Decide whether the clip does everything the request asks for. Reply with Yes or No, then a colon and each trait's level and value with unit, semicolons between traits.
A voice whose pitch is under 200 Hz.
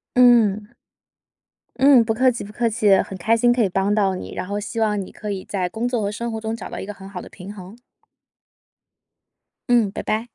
No: high, 215 Hz